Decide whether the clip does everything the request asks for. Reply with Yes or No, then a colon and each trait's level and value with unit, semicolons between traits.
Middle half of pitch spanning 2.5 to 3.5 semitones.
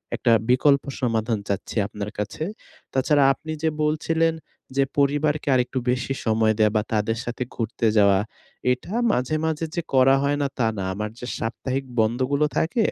No: average, 4.6 semitones